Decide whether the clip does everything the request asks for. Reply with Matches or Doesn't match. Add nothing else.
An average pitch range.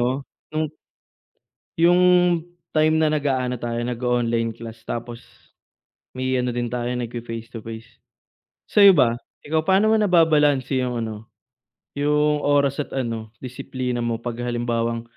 Matches